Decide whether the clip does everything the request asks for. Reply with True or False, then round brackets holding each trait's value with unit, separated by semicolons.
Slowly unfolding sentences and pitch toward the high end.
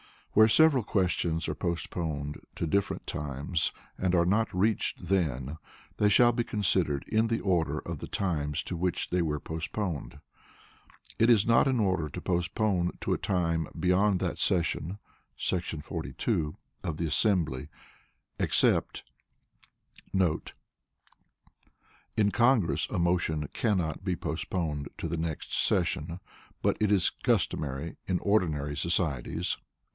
False (130 wpm; 85 Hz)